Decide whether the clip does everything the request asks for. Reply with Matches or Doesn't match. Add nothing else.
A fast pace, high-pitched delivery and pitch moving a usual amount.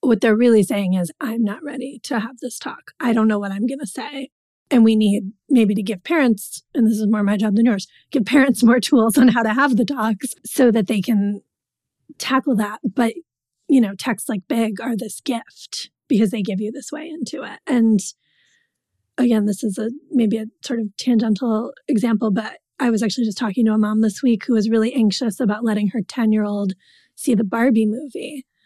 Matches